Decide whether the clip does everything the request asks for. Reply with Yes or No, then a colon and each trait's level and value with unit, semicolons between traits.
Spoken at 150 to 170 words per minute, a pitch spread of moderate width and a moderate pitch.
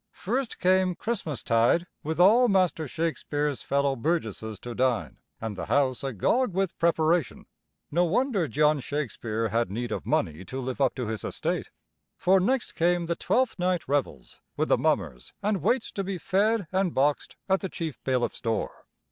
No: average, 165 wpm; wide, 6.7 semitones; medium, 160 Hz